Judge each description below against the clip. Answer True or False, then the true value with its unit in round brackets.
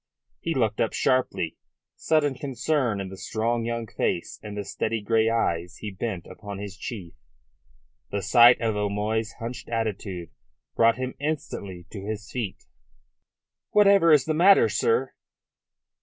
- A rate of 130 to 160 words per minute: True (140 wpm)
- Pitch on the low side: True (115 Hz)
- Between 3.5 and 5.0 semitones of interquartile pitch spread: True (4.0 semitones)